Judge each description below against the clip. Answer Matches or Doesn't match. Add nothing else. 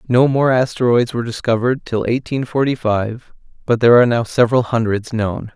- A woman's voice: Doesn't match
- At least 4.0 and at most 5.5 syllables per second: Doesn't match